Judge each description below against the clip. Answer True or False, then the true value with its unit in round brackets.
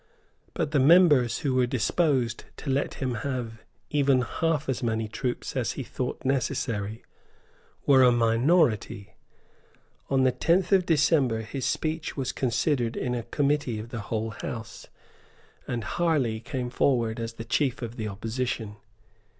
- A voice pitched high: False (125 Hz)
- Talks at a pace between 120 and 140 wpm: False (150 wpm)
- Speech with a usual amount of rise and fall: True (3.9 semitones)